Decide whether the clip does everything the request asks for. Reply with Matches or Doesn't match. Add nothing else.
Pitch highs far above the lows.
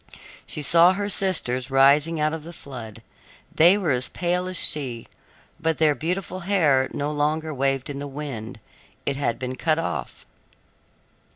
Doesn't match